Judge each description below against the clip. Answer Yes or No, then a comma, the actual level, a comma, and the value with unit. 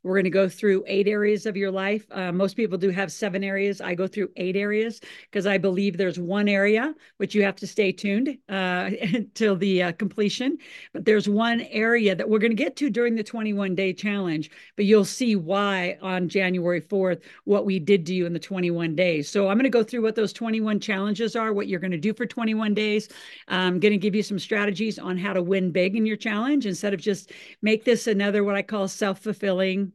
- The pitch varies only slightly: Yes, narrow, 2.2 semitones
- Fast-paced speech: Yes, fast, 230 wpm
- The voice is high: Yes, high, 200 Hz